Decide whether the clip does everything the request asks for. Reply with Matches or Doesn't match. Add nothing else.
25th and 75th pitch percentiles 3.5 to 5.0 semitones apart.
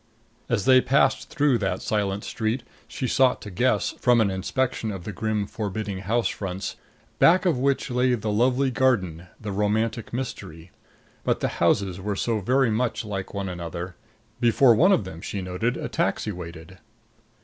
Matches